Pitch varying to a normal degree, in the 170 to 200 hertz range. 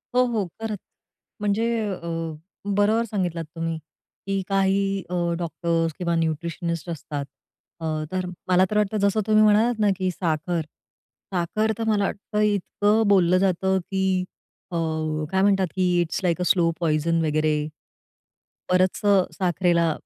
Yes: average, 3.3 semitones; medium, 185 Hz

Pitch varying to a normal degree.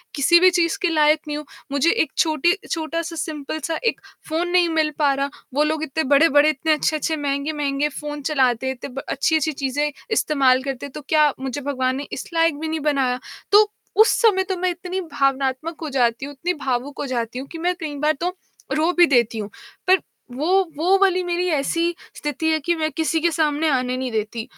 Yes: average, 3.3 semitones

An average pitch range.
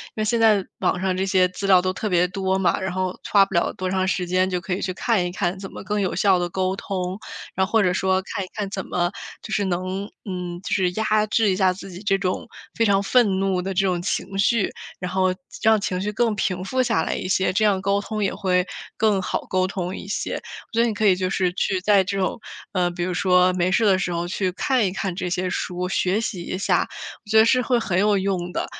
No: narrow, 1.8 semitones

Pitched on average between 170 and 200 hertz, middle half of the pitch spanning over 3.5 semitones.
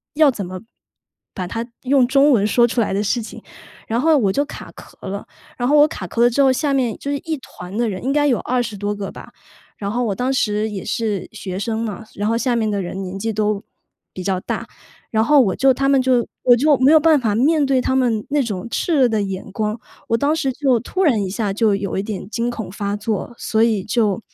No: high, 230 Hz; average, 4.5 semitones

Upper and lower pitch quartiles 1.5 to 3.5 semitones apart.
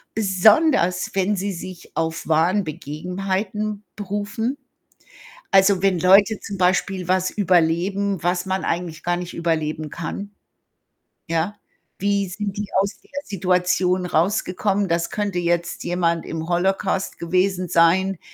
Yes: narrow, 2.6 semitones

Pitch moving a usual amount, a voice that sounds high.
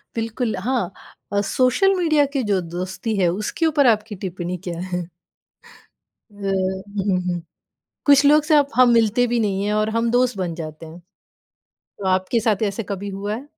Yes: average, 4.7 semitones; high, 210 Hz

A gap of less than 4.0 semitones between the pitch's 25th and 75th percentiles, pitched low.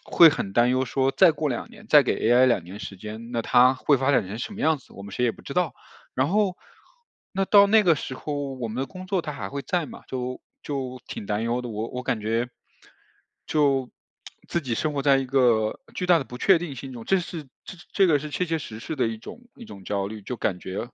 No: average, 5.3 semitones; low, 130 Hz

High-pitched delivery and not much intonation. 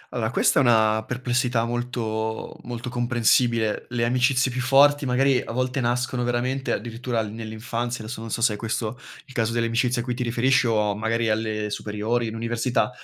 No: low, 120 Hz; narrow, 1.9 semitones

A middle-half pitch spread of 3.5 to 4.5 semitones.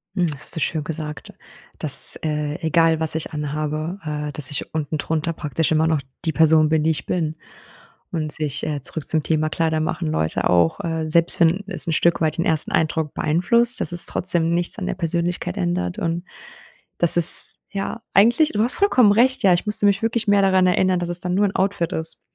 No: average, 2.9 semitones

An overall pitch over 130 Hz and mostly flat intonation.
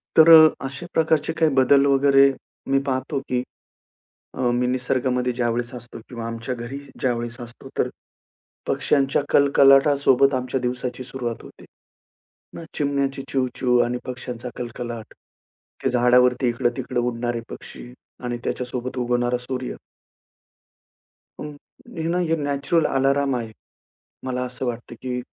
No: low, 125 Hz; narrow, 2.0 semitones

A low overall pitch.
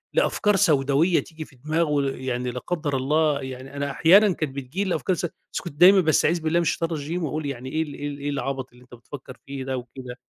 No: medium, 145 Hz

